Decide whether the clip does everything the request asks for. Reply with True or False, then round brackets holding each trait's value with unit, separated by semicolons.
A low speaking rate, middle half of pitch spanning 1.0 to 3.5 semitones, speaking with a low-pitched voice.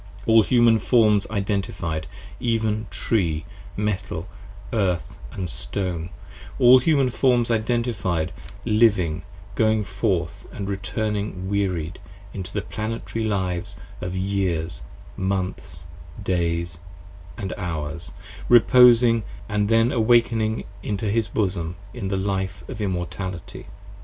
False (110 wpm; 3.9 semitones; 100 Hz)